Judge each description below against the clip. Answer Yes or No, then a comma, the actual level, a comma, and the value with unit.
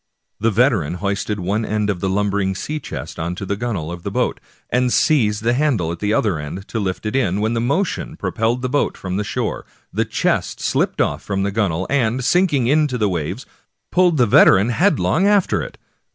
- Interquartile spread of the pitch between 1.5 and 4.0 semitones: No, average, 4.8 semitones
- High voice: No, low, 105 Hz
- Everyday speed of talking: No, fast, 215 wpm